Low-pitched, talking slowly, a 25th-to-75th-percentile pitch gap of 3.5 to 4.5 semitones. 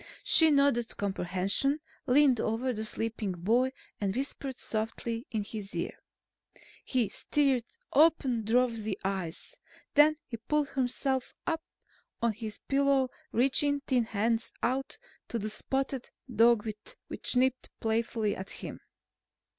No: high, 235 Hz; slow, 125 wpm; average, 3.8 semitones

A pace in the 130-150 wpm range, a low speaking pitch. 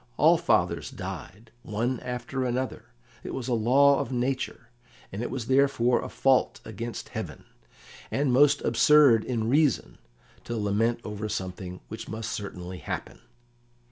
Yes: average, 140 wpm; low, 120 Hz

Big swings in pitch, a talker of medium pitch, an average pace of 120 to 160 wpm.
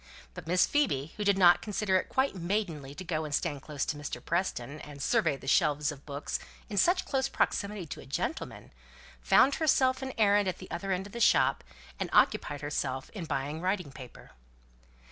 No: wide, 5.9 semitones; medium, 175 Hz; average, 195 wpm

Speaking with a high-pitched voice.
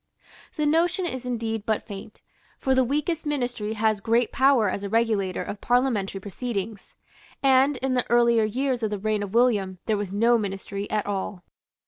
Yes: high, 225 Hz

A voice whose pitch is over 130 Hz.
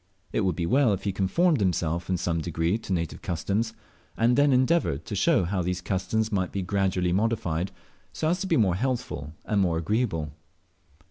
No: very low, 95 Hz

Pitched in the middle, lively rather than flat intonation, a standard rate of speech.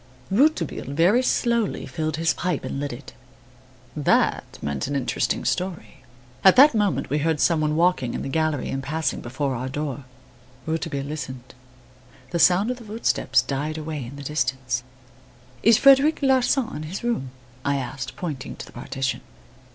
Yes: medium, 155 Hz; wide, 5.8 semitones; average, 165 wpm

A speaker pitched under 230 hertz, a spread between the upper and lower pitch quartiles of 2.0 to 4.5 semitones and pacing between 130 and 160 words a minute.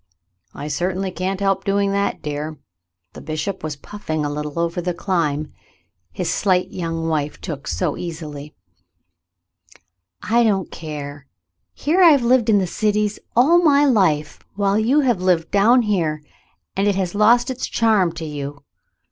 No: medium, 185 Hz; average, 5.3 semitones; average, 150 wpm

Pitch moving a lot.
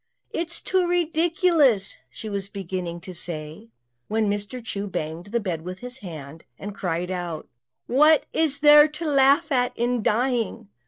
Yes: wide, 8.1 semitones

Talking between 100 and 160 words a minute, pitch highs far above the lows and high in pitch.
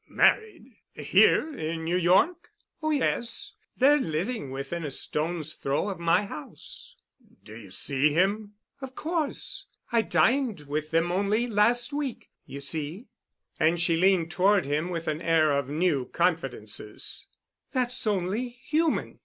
No: average, 140 wpm; wide, 7.7 semitones; medium, 180 Hz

